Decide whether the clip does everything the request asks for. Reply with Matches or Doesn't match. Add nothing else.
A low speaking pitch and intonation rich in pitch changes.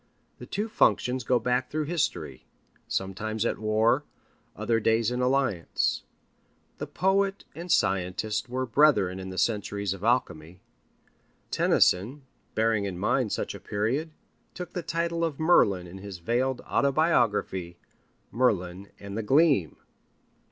Matches